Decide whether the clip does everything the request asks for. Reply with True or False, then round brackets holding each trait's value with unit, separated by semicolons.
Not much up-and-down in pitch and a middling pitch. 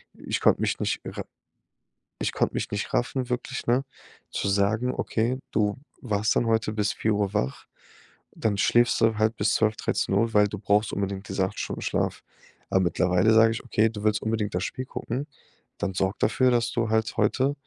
False (2.1 semitones; 110 Hz)